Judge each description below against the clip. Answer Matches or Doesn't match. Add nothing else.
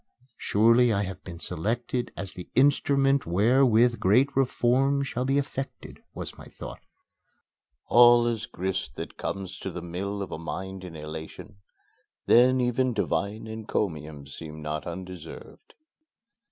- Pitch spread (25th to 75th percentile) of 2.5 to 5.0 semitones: Doesn't match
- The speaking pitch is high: Doesn't match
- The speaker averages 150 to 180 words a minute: Doesn't match